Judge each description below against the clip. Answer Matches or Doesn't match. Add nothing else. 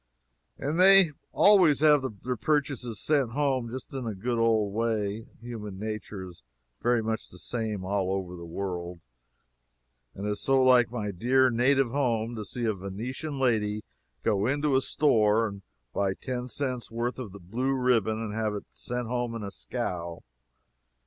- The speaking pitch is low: Matches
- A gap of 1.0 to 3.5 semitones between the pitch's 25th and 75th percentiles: Doesn't match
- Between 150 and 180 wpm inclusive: Matches